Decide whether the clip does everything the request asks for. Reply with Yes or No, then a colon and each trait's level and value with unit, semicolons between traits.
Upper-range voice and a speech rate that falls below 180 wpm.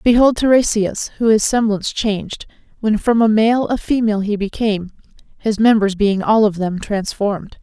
Yes: high, 215 Hz; average, 165 wpm